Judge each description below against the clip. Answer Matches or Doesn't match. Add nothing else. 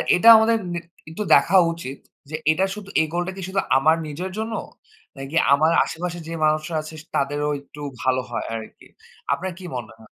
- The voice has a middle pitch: Matches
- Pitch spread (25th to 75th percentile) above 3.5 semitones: Matches